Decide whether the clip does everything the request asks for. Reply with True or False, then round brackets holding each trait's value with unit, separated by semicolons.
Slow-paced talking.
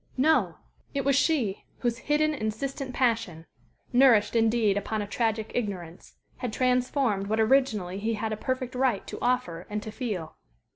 False (155 wpm)